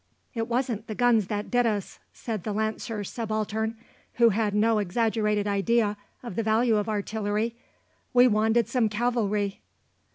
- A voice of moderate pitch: No, high, 220 Hz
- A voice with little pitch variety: Yes, narrow, 2.0 semitones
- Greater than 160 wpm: No, average, 150 wpm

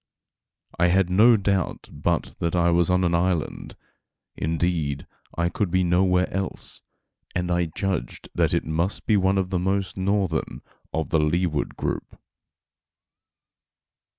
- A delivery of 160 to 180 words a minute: No, average, 140 wpm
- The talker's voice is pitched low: Yes, very low, 90 Hz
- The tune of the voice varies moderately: No, narrow, 2.1 semitones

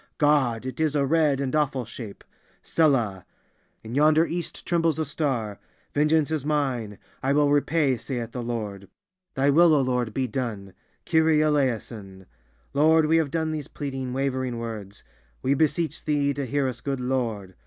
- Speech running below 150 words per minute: Yes, average, 140 wpm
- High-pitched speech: No, low, 135 Hz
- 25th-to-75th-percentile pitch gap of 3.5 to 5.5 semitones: Yes, average, 4.6 semitones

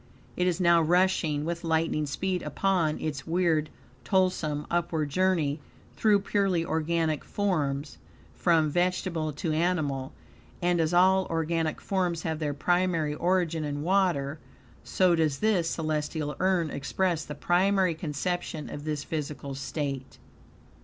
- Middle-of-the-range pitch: Yes, medium, 165 Hz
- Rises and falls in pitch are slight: No, average, 3.1 semitones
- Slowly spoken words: Yes, slow, 130 wpm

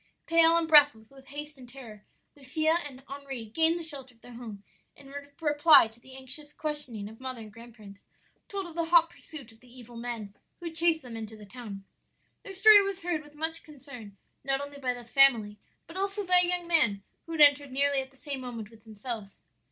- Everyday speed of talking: No, fast, 215 wpm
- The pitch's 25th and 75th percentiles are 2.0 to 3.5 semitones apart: No, wide, 5.6 semitones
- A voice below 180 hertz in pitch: No, very high, 275 Hz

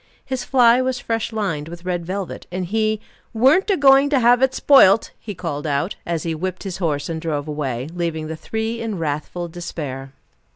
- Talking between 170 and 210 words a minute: Yes, average, 195 wpm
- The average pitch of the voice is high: No, medium, 180 Hz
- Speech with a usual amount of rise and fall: No, wide, 6.3 semitones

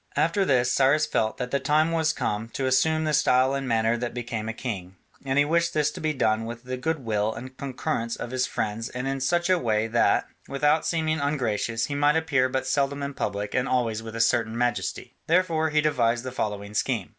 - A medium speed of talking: No, fast, 215 wpm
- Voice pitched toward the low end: Yes, low, 130 Hz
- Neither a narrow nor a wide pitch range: Yes, average, 4.6 semitones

